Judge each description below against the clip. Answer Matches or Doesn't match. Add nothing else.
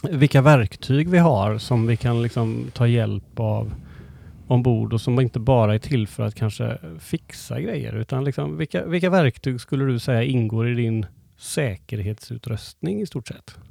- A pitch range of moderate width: Matches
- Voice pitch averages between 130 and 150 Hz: Doesn't match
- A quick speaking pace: Doesn't match